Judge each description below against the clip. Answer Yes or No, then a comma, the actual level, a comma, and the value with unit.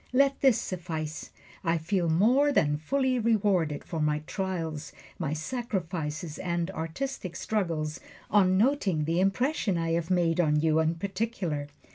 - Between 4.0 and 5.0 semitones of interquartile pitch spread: Yes, average, 4.6 semitones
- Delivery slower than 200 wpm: Yes, average, 140 wpm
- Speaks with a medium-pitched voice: Yes, medium, 175 Hz